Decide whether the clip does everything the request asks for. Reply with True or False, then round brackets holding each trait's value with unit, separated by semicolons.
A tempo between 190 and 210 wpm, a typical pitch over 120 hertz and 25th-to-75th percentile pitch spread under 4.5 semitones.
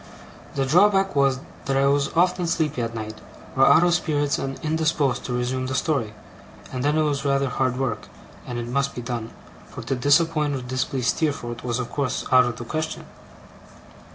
True (195 wpm; 135 Hz; 3.5 semitones)